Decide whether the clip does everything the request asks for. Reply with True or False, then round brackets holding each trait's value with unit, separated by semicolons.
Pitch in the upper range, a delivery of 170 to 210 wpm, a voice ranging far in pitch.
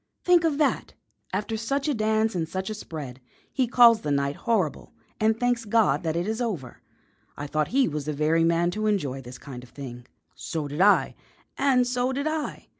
True (205 Hz; 200 wpm; 8.2 semitones)